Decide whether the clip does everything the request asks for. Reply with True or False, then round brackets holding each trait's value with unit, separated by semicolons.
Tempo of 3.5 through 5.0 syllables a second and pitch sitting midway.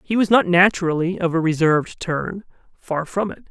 False (5.4 syllables/s; 180 Hz)